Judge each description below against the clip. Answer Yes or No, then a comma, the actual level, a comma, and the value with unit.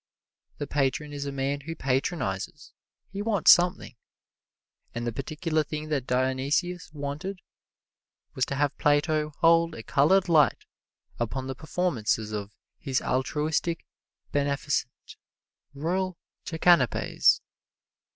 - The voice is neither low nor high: Yes, medium, 145 Hz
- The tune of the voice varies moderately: Yes, average, 3.8 semitones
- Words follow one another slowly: Yes, slow, 110 wpm